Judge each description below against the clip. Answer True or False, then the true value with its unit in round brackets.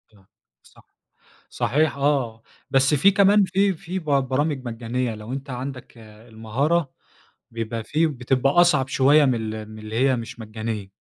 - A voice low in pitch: True (130 Hz)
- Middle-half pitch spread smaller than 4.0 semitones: False (4.8 semitones)